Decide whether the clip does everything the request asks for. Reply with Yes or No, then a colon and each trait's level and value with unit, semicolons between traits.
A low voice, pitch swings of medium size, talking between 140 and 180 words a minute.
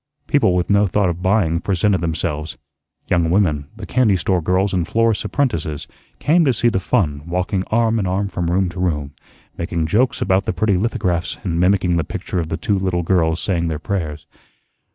No: very low, 90 Hz; average, 3.4 semitones; average, 195 wpm